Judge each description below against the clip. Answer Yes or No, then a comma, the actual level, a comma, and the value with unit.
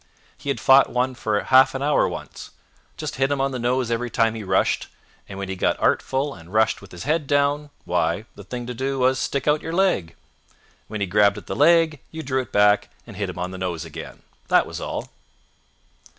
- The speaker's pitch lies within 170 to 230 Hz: No, low, 125 Hz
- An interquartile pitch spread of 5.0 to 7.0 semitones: Yes, wide, 5.4 semitones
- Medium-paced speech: No, fast, 225 wpm